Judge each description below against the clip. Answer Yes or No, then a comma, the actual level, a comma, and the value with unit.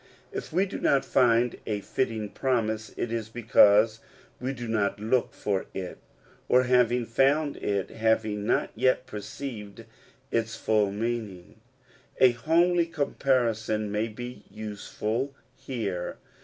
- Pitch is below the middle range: Yes, low, 115 Hz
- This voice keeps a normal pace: No, slow, 130 wpm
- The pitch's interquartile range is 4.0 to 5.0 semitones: No, average, 3.2 semitones